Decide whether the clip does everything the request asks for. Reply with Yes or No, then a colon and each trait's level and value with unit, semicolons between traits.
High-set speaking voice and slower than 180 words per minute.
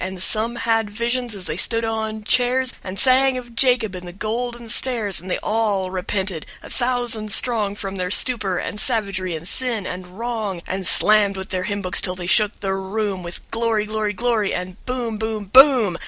No: high, 215 Hz; average, 195 wpm